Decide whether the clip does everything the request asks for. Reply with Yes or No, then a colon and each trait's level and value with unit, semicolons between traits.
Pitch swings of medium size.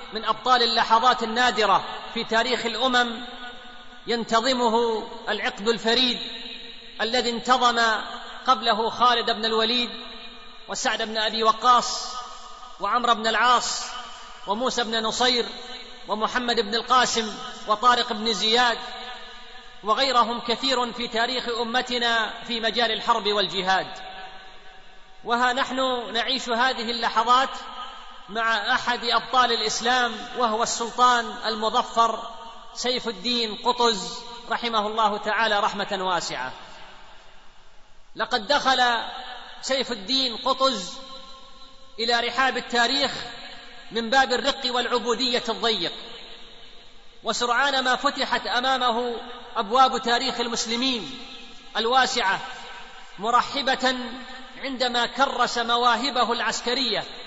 No: narrow, 1.5 semitones